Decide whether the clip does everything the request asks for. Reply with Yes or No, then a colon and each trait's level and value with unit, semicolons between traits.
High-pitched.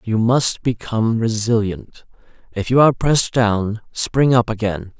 No: low, 115 Hz